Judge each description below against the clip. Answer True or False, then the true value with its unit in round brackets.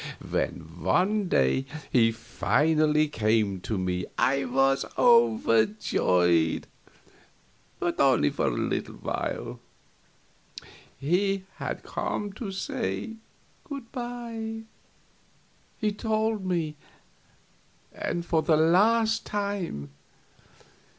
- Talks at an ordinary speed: False (90 wpm)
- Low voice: False (165 Hz)